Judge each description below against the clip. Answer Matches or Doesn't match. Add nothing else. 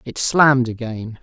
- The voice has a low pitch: Matches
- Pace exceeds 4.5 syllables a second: Doesn't match